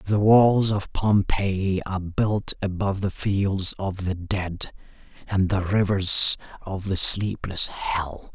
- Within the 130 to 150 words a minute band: Yes, slow, 135 wpm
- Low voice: Yes, very low, 95 Hz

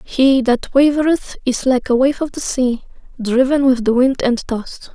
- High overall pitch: Yes, very high, 260 Hz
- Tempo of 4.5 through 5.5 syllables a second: Yes, 4.6 syllables/s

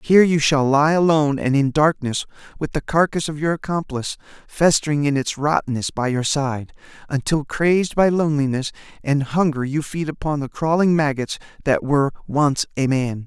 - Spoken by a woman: No, male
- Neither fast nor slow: Yes, average, 170 wpm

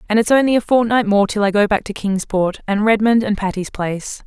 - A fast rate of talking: Yes, fast, 240 wpm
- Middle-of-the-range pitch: No, high, 210 Hz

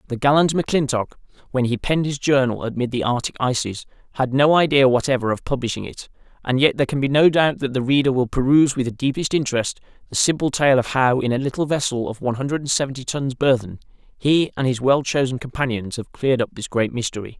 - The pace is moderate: No, fast, 215 wpm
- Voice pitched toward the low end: Yes, low, 130 Hz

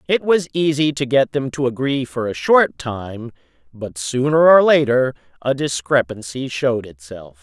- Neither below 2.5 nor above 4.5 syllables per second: Yes, 4.4 syllables/s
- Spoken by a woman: No, male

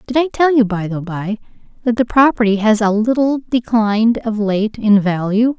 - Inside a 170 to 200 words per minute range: Yes, average, 195 wpm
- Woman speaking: Yes, female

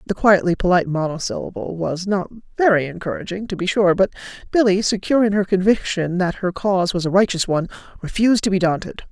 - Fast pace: No, average, 185 wpm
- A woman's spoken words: Yes, female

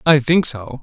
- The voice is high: No, medium, 140 Hz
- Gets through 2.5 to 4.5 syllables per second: Yes, 4.2 syllables/s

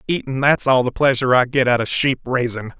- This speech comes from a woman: No, male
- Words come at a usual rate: No, fast, 215 wpm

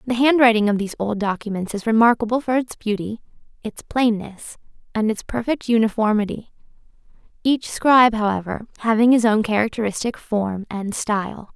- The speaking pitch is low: No, high, 220 Hz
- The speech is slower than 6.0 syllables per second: Yes, 5.4 syllables/s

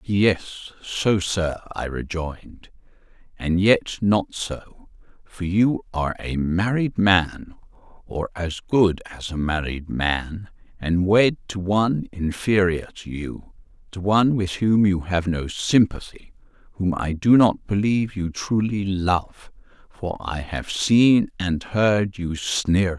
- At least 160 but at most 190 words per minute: No, slow, 135 wpm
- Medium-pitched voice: No, very low, 95 Hz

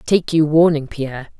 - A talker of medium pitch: Yes, medium, 155 Hz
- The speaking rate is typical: Yes, average, 170 wpm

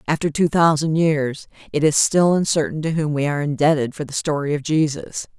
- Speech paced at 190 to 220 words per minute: Yes, average, 200 wpm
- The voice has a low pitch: No, medium, 150 Hz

